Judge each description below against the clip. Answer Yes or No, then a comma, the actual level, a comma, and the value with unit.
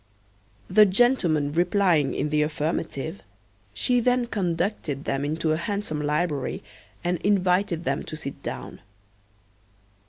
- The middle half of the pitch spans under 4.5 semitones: No, average, 4.9 semitones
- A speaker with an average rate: No, slow, 120 wpm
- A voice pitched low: No, medium, 170 Hz